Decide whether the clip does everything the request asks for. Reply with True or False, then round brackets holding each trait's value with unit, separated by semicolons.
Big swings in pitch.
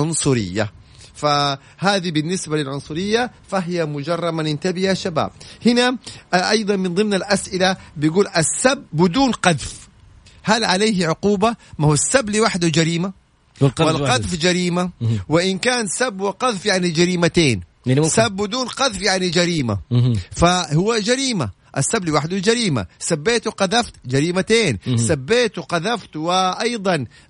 True (6.0 semitones)